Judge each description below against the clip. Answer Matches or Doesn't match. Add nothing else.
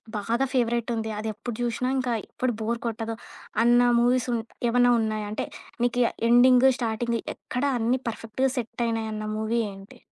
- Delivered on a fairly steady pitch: Matches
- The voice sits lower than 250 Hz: Matches